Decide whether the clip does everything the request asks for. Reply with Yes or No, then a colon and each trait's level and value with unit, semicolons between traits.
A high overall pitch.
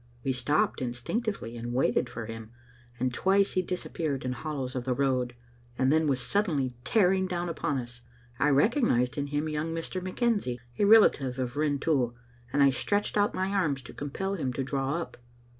No: medium, 145 Hz